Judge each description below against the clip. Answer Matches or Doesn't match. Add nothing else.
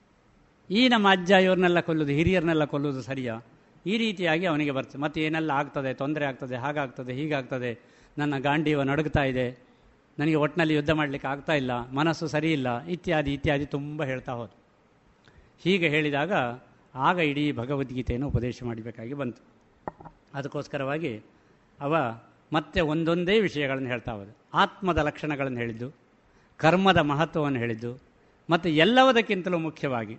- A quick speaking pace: Matches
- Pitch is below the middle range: Doesn't match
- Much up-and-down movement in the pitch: Doesn't match